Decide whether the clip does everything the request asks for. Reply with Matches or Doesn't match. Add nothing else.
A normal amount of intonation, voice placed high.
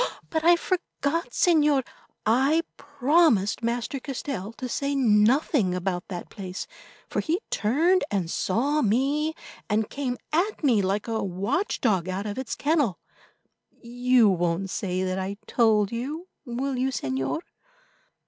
Doesn't match